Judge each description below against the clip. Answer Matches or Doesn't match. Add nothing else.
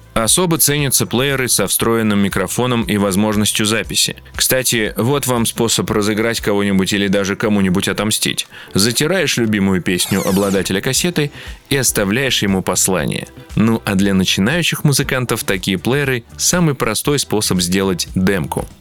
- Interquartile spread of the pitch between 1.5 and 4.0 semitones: Doesn't match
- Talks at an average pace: Matches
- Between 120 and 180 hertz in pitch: Doesn't match